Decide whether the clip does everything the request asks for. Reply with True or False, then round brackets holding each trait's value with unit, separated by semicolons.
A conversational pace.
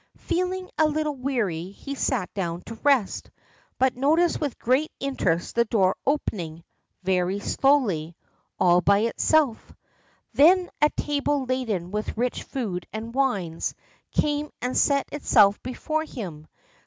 False (130 wpm)